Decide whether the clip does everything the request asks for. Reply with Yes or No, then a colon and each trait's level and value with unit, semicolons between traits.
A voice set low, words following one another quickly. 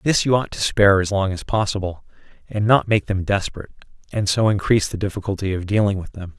Yes: low, 100 Hz; fast, 215 wpm